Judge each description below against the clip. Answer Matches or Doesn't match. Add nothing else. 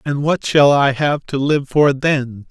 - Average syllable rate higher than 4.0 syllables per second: Doesn't match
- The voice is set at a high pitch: Doesn't match